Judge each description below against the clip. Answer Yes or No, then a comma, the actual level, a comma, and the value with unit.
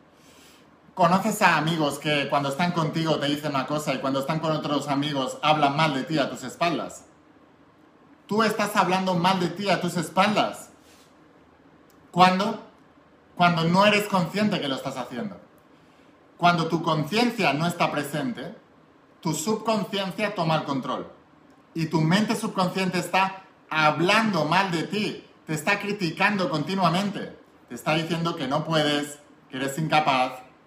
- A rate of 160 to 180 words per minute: No, average, 145 wpm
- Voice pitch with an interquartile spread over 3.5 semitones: Yes, average, 4.3 semitones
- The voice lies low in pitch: No, medium, 170 Hz